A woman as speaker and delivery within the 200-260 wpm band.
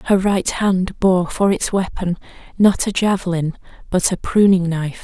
No: female; average, 165 wpm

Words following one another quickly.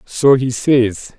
No: average, 150 wpm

